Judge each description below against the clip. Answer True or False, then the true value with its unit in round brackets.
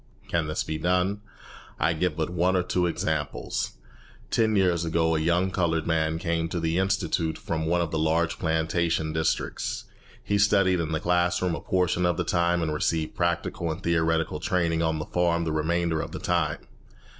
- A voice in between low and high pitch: False (85 Hz)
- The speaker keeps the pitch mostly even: True (1.7 semitones)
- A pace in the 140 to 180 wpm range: False (190 wpm)